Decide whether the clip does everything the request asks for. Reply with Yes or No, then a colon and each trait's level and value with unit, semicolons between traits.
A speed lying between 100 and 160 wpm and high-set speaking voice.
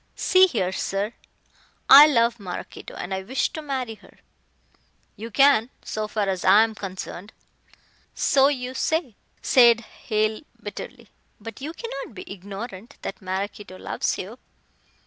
Yes: average, 140 wpm; high, 220 Hz